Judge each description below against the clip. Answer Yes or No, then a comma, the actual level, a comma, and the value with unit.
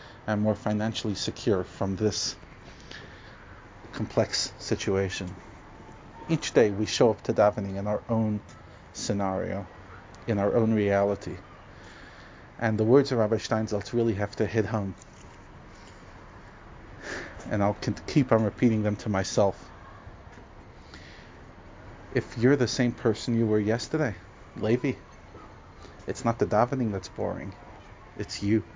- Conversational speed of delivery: No, slow, 125 wpm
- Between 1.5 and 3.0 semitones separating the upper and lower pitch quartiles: Yes, narrow, 2.5 semitones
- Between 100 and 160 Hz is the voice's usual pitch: Yes, low, 105 Hz